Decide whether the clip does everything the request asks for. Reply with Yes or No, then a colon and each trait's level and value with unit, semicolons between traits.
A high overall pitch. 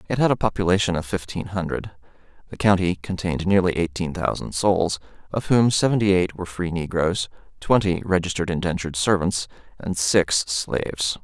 No: very low, 90 Hz